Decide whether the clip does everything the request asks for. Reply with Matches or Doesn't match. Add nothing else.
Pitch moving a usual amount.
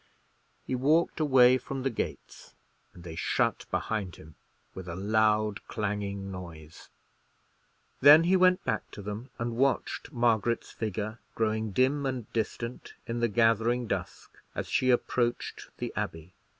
Matches